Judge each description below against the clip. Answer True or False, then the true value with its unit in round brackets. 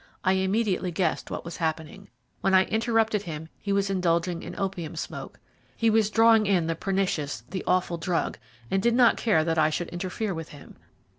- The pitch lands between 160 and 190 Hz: True (185 Hz)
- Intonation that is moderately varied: True (3.8 semitones)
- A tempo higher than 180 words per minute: True (190 wpm)